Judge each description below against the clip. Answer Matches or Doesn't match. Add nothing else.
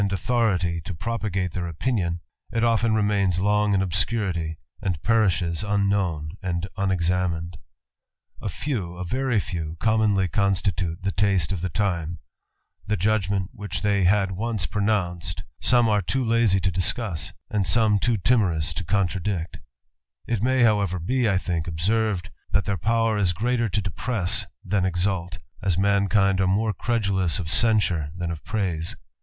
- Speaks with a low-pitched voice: Matches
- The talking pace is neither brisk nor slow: Doesn't match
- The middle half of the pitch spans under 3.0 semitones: Doesn't match